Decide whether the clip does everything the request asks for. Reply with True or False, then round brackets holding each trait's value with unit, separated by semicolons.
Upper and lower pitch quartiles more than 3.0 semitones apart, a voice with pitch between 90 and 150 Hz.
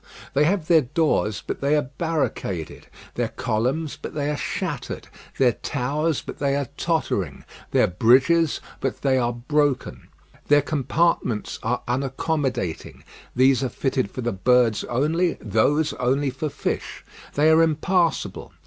True (4.0 semitones; 140 Hz)